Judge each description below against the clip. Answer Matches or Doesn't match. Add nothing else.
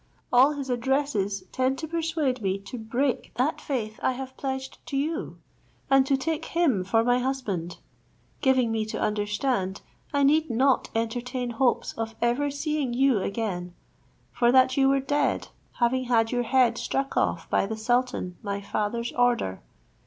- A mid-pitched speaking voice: Doesn't match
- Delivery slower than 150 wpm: Doesn't match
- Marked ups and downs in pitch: Doesn't match